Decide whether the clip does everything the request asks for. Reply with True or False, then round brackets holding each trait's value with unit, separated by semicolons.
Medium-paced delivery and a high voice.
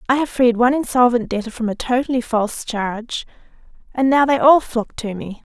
True (195 wpm; 240 Hz)